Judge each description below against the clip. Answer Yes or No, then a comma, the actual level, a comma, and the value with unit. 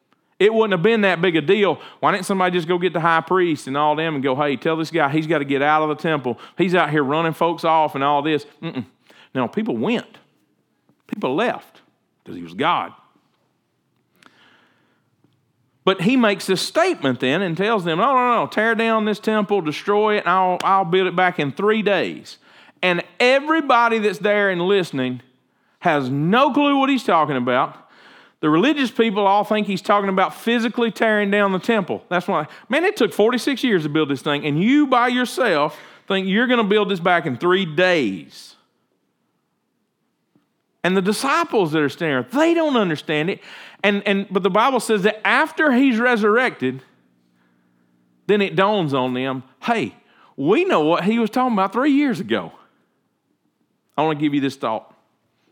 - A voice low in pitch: No, high, 190 Hz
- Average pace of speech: Yes, average, 190 wpm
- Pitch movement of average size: No, wide, 6.4 semitones